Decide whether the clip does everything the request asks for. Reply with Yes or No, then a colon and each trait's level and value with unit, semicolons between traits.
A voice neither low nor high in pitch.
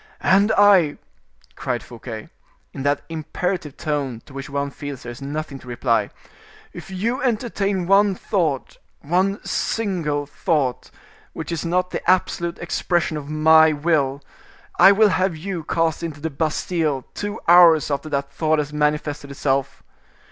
Yes: medium, 155 Hz